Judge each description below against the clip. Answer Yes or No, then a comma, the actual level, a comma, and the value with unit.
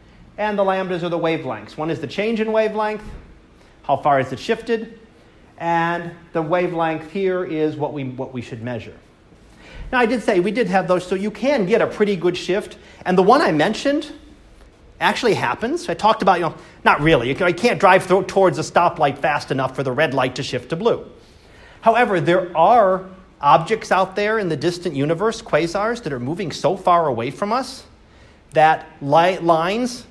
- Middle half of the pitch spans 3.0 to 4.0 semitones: No, average, 5.0 semitones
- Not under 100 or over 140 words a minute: No, average, 195 wpm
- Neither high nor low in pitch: Yes, medium, 180 Hz